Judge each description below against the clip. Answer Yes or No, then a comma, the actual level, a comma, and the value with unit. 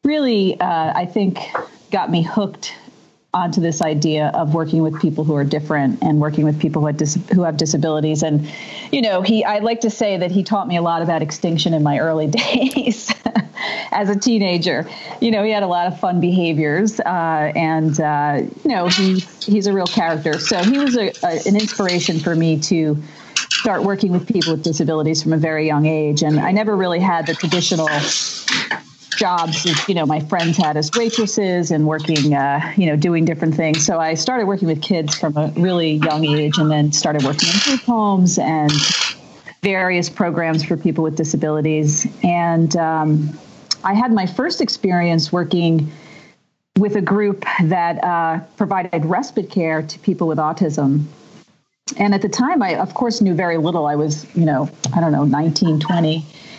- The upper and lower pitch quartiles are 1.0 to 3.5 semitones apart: No, average, 4.2 semitones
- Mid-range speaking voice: Yes, medium, 170 Hz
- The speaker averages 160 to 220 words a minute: Yes, average, 190 wpm